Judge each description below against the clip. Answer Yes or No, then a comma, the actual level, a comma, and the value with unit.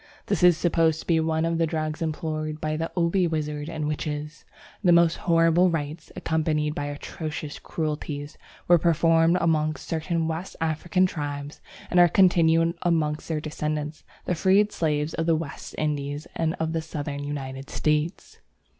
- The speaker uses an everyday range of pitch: No, narrow, 1.7 semitones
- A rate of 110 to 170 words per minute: Yes, average, 160 wpm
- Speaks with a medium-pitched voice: Yes, medium, 160 Hz